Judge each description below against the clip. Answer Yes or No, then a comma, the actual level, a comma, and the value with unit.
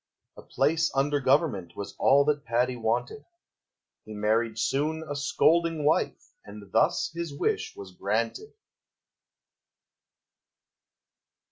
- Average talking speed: No, slow, 110 wpm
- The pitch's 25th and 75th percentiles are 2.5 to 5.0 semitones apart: No, wide, 5.5 semitones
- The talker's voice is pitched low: Yes, low, 130 Hz